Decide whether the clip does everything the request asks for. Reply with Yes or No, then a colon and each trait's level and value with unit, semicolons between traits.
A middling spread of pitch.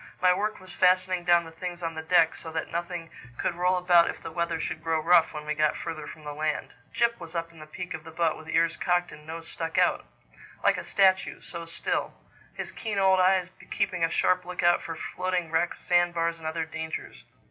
No: narrow, 2.0 semitones